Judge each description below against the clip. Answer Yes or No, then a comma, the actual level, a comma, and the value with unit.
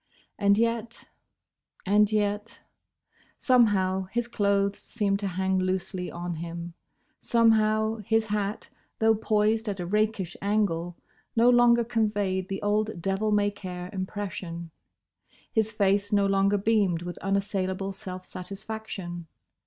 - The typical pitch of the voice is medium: No, high, 200 Hz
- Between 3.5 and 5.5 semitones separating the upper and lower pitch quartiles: No, narrow, 2.5 semitones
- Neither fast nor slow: No, slow, 120 wpm